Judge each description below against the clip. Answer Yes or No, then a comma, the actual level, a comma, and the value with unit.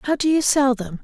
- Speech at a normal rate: No, fast, 290 wpm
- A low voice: No, very high, 265 Hz